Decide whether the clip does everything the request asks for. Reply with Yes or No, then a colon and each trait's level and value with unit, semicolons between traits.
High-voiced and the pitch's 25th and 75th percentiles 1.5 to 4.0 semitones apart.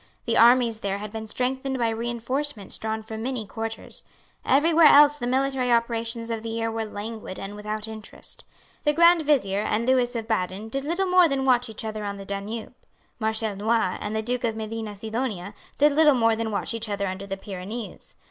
Yes: high, 225 Hz; average, 3.0 semitones